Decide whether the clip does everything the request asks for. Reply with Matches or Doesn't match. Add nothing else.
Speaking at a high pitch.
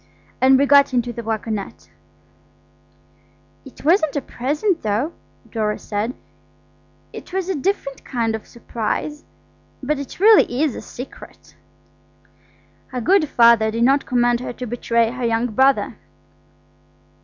Matches